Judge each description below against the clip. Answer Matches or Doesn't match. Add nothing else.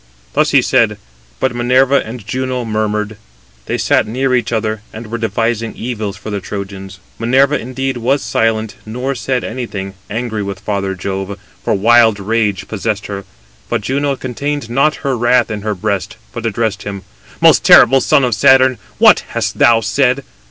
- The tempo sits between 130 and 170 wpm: Matches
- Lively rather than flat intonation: Doesn't match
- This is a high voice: Doesn't match